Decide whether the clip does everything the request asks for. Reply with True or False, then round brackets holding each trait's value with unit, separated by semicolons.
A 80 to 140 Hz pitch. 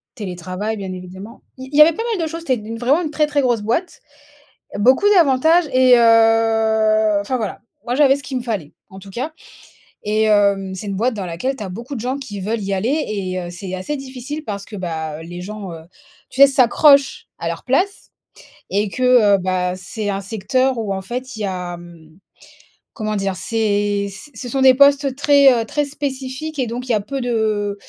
False (225 Hz)